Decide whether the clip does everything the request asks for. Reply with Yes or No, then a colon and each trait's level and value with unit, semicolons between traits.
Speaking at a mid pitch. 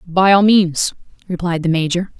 Yes: medium, 180 Hz